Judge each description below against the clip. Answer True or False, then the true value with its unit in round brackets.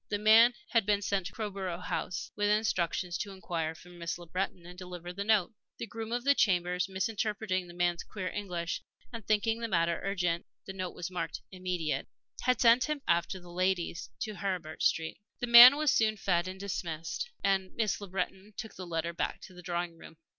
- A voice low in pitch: False (185 Hz)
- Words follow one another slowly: False (200 wpm)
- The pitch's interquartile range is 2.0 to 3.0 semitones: False (3.5 semitones)